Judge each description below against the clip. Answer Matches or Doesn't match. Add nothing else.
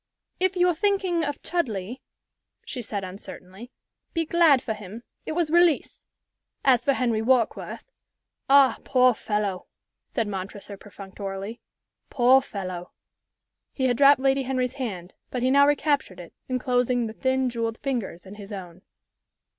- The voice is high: Matches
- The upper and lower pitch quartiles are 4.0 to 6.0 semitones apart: Matches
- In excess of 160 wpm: Doesn't match